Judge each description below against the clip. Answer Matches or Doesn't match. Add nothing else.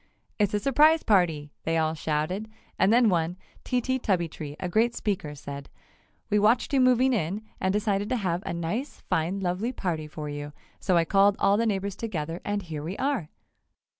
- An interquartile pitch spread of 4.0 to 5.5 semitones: Matches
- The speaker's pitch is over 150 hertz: Matches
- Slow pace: Doesn't match